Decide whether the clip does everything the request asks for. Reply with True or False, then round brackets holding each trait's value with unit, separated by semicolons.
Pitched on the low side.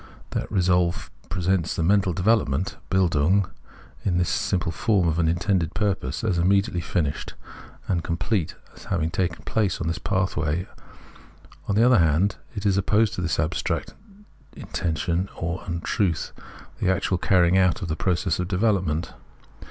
True (90 Hz)